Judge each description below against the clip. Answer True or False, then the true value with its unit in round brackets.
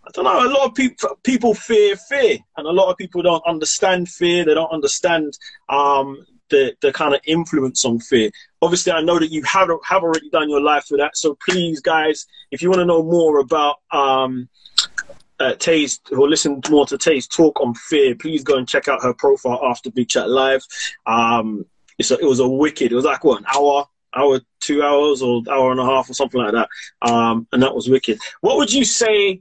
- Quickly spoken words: True (220 wpm)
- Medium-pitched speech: True (155 Hz)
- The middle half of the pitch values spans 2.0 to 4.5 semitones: False (5.6 semitones)